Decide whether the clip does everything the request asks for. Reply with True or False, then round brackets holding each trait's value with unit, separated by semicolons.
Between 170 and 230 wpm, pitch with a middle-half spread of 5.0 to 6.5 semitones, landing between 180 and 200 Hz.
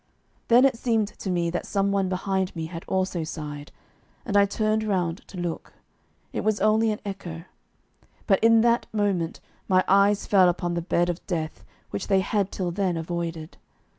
False (180 wpm; 3.2 semitones; 190 Hz)